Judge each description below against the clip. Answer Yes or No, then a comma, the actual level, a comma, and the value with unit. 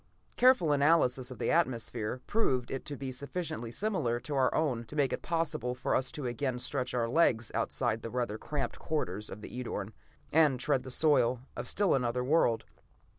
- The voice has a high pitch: No, low, 130 Hz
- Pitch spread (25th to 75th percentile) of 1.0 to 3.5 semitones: No, average, 4.0 semitones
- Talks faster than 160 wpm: Yes, average, 185 wpm